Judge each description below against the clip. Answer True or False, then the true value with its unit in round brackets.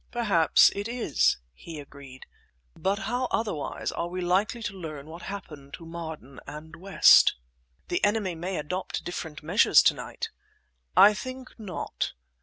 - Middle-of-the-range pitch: True (175 Hz)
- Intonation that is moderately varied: True (4.9 semitones)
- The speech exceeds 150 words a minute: False (145 wpm)